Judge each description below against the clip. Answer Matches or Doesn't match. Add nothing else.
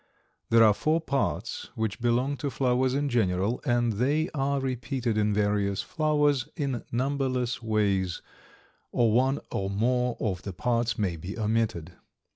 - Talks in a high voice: Doesn't match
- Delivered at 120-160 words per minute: Matches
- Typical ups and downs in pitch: Matches